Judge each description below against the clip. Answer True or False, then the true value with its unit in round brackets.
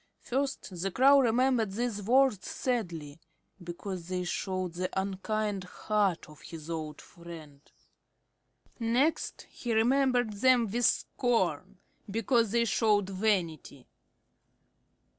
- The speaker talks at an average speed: False (105 wpm)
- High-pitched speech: True (205 Hz)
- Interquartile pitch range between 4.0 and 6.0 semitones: True (5.1 semitones)